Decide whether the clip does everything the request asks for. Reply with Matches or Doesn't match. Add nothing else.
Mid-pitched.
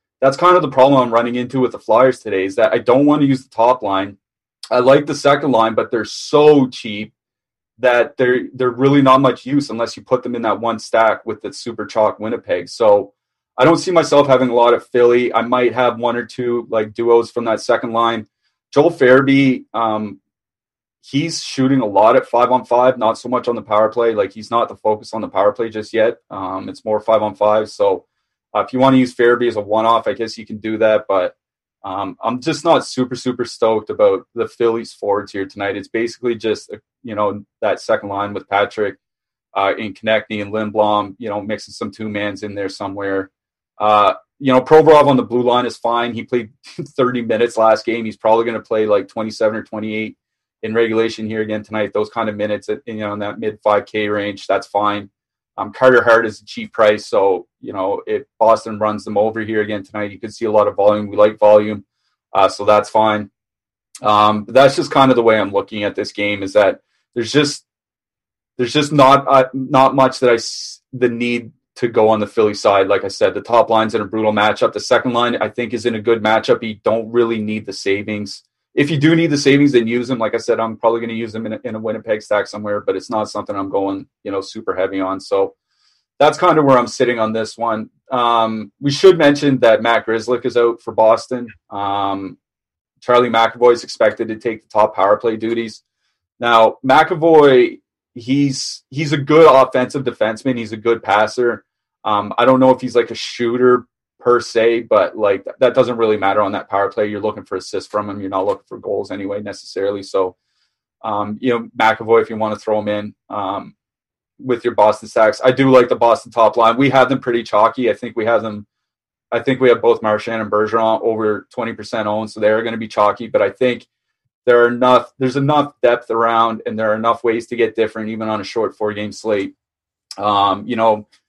Doesn't match